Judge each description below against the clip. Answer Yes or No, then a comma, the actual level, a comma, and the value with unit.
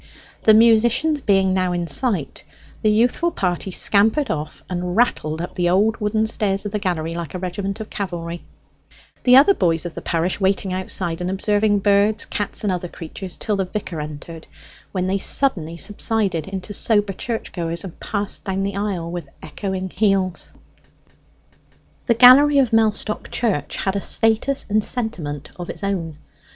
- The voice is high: Yes, high, 195 Hz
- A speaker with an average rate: Yes, average, 165 wpm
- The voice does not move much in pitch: No, average, 3.6 semitones